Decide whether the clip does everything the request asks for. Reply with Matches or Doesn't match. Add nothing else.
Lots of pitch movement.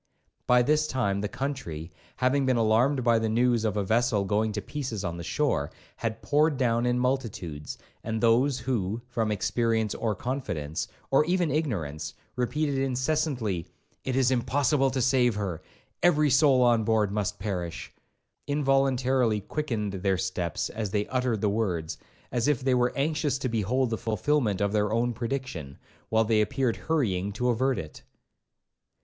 Doesn't match